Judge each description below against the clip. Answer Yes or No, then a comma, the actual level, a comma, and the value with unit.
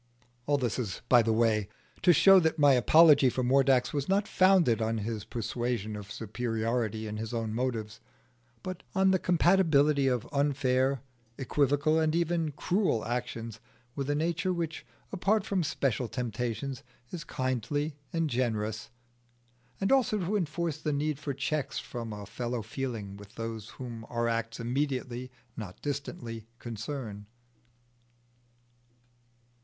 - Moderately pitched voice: No, low, 130 Hz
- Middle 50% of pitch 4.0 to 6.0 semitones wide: Yes, average, 5.2 semitones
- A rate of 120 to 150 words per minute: Yes, average, 140 wpm